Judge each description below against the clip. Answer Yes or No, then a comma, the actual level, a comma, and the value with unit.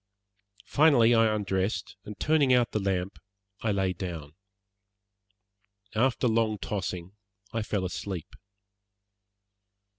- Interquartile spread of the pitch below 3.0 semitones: No, average, 3.6 semitones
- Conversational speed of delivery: No, slow, 100 wpm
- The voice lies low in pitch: Yes, low, 105 Hz